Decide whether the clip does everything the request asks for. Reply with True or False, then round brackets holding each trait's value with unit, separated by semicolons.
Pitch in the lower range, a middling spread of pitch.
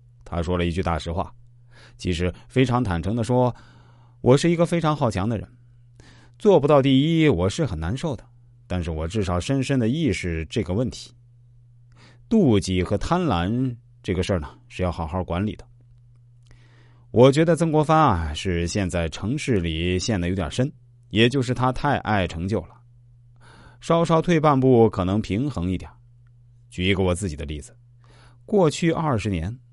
True (120 Hz; 5.0 semitones)